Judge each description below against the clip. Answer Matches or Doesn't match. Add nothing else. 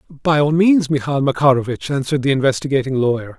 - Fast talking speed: Doesn't match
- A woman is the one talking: Doesn't match